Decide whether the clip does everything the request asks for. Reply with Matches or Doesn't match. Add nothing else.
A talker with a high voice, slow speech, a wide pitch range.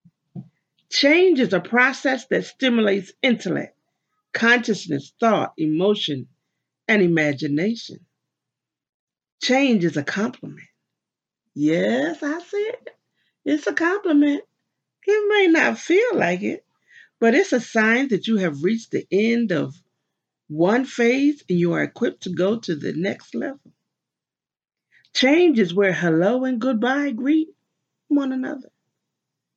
Matches